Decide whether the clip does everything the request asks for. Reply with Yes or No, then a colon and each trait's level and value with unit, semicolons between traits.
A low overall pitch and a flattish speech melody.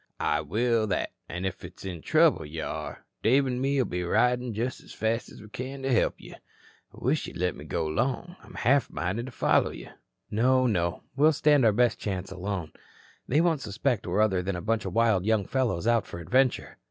No: low, 115 Hz; wide, 5.5 semitones